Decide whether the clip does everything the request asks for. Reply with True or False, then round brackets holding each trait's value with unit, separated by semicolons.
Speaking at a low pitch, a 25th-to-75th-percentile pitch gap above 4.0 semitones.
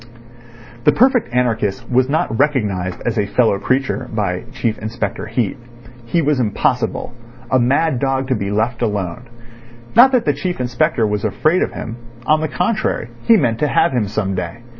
True (120 Hz; 4.6 semitones)